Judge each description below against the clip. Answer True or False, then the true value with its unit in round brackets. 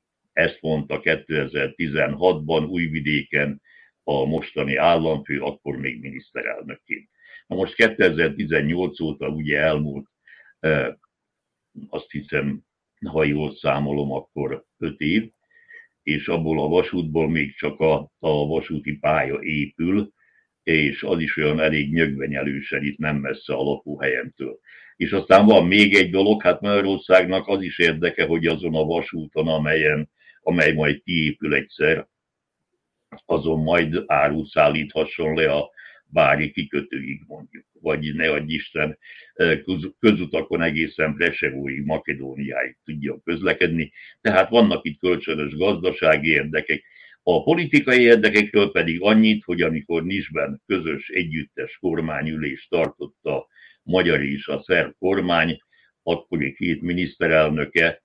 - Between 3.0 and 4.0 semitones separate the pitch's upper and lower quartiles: True (3.3 semitones)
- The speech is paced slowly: False (115 wpm)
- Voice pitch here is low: True (80 Hz)